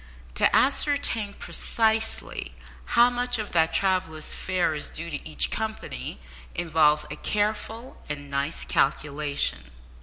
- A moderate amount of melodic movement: No, wide, 6.7 semitones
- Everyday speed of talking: No, slow, 120 wpm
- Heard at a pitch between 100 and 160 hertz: No, medium, 175 Hz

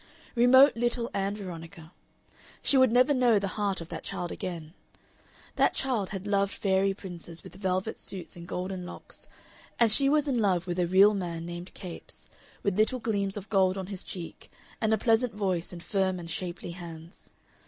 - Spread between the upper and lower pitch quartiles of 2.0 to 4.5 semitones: Yes, average, 3.7 semitones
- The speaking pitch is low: No, high, 195 Hz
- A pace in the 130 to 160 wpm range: No, average, 185 wpm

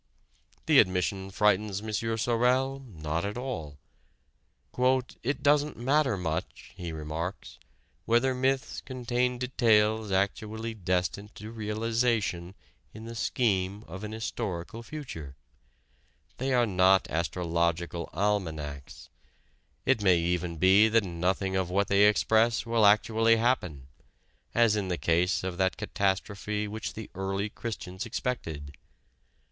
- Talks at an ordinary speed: No, slow, 120 wpm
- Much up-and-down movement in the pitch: No, average, 4.3 semitones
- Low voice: Yes, low, 105 Hz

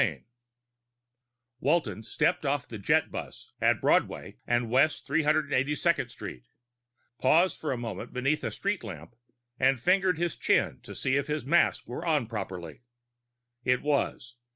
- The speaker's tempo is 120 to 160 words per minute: Yes, average, 140 wpm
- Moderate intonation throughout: Yes, average, 4.7 semitones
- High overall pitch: No, low, 135 Hz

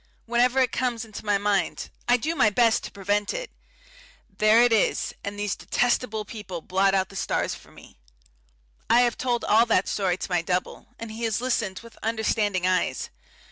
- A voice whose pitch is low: No, high, 215 Hz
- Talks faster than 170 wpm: Yes, average, 185 wpm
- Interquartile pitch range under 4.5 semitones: Yes, average, 3.3 semitones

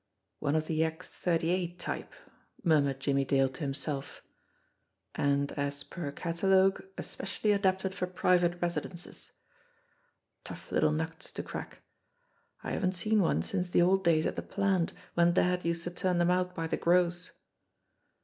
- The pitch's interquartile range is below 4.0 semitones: Yes, average, 2.7 semitones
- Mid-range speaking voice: Yes, medium, 175 Hz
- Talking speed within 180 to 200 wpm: No, average, 155 wpm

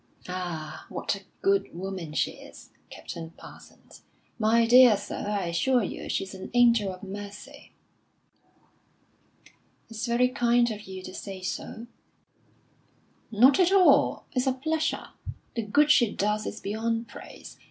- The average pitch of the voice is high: Yes, high, 210 Hz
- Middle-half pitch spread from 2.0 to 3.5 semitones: No, average, 4.0 semitones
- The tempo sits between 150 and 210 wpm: No, average, 140 wpm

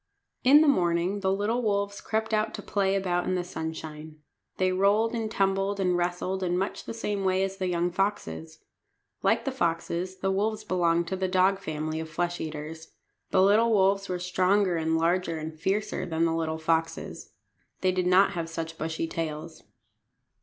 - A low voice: No, medium, 185 Hz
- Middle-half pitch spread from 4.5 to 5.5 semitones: No, average, 3.1 semitones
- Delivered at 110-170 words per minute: No, average, 180 wpm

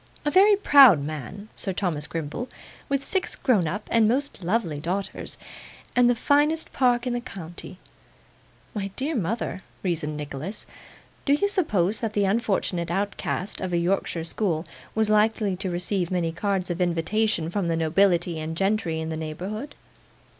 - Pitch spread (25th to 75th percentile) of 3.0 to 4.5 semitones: No, average, 5.2 semitones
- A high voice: Yes, high, 195 Hz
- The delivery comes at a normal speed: Yes, average, 160 wpm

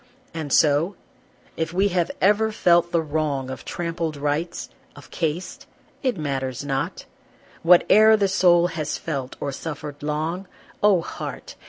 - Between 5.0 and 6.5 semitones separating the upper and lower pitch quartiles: No, average, 3.6 semitones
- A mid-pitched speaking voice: Yes, medium, 165 Hz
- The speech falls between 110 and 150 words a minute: Yes, average, 145 wpm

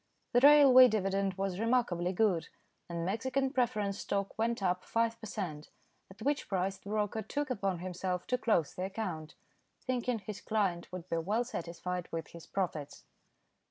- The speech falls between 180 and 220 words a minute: No, average, 160 wpm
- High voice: Yes, high, 195 Hz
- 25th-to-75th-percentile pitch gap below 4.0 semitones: No, average, 4.3 semitones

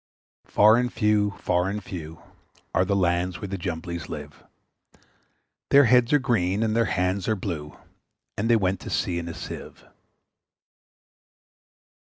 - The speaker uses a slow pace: No, average, 150 wpm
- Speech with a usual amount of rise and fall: Yes, average, 3.8 semitones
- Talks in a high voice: No, very low, 95 Hz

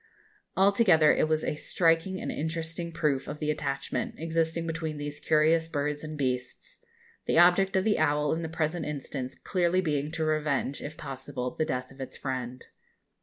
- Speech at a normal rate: Yes, average, 170 wpm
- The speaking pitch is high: No, medium, 155 Hz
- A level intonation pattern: Yes, narrow, 2.3 semitones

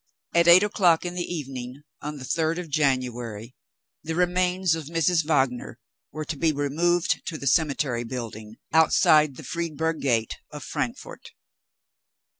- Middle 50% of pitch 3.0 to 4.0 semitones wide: No, average, 4.5 semitones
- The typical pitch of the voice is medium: Yes, medium, 155 Hz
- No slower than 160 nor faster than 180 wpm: No, average, 145 wpm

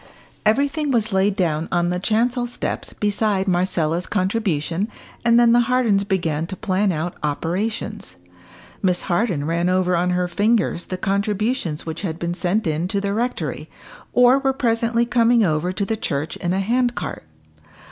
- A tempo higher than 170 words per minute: No, average, 165 wpm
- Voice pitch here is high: Yes, high, 195 Hz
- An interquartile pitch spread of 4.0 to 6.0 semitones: Yes, average, 4.7 semitones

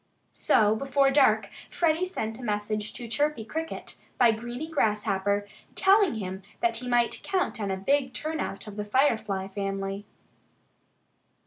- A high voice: Yes, high, 225 Hz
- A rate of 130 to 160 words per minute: Yes, average, 140 wpm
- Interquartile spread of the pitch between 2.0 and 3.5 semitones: No, wide, 5.4 semitones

